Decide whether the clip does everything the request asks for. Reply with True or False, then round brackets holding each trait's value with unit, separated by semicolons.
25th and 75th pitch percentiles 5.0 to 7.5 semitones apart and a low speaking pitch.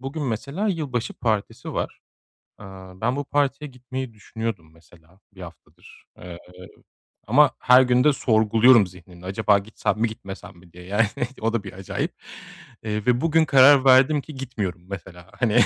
True (5.5 semitones; 110 Hz)